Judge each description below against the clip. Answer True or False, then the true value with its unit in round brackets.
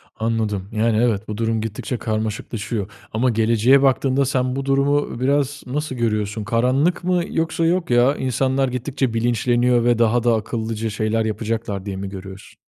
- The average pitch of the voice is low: True (115 Hz)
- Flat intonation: False (3.3 semitones)